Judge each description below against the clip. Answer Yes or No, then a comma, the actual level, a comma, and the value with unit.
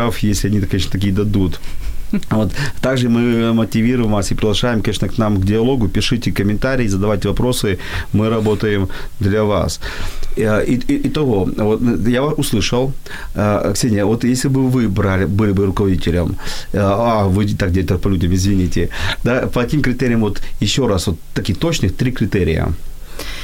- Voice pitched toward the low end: Yes, low, 105 Hz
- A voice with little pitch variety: No, average, 3.8 semitones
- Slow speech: No, average, 150 wpm